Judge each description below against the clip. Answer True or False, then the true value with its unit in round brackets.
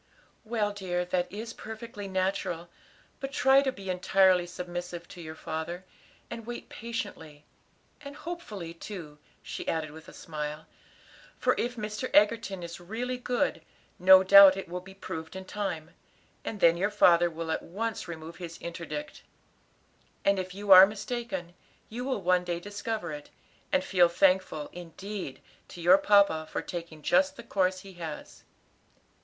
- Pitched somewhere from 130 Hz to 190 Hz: True (185 Hz)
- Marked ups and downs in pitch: False (3.8 semitones)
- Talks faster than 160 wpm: False (155 wpm)